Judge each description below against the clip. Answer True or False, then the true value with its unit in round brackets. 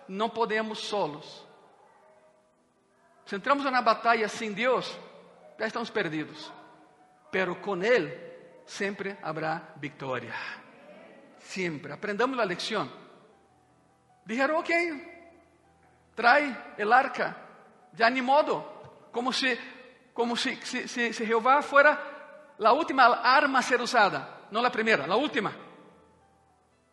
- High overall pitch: True (235 Hz)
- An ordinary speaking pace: False (115 wpm)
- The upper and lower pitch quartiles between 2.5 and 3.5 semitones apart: False (5.6 semitones)